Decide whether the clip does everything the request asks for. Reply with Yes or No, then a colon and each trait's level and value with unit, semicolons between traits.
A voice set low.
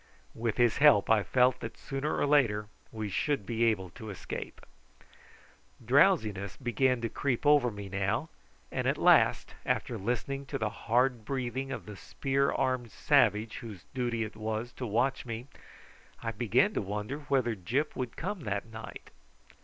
Yes: low, 120 Hz